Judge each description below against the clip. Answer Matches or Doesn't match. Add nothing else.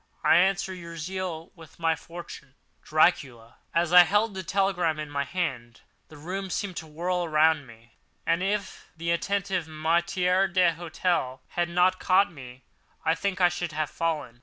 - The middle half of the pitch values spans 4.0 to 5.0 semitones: Doesn't match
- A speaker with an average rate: Matches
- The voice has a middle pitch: Matches